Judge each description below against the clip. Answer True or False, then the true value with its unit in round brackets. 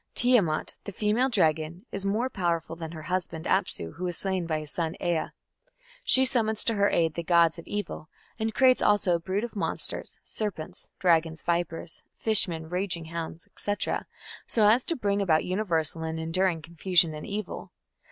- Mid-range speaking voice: True (175 Hz)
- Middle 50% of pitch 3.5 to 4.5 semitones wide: True (4.1 semitones)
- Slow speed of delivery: False (175 wpm)